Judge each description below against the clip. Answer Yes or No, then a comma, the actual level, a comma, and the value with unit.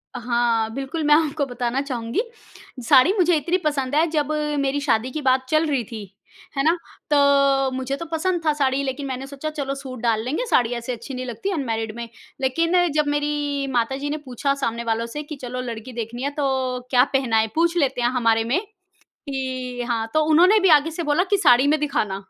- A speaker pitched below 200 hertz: No, very high, 270 Hz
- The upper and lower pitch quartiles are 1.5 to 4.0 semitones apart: Yes, average, 3.5 semitones